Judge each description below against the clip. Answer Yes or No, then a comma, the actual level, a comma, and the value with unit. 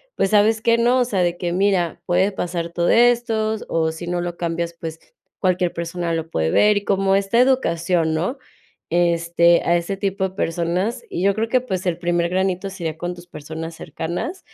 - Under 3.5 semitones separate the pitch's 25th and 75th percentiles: Yes, average, 2.8 semitones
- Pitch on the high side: No, medium, 175 Hz